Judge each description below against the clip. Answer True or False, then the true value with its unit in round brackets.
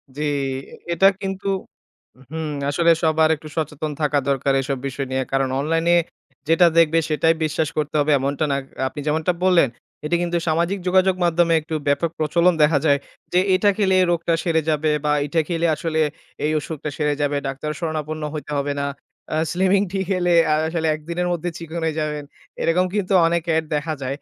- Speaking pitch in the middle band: True (160 Hz)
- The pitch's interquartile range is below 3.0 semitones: True (2.4 semitones)